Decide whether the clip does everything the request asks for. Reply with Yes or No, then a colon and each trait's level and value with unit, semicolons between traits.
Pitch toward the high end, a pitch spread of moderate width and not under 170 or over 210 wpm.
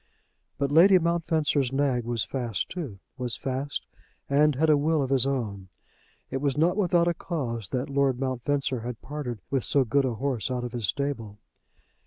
No: low, 135 Hz; average, 3.4 semitones; average, 180 wpm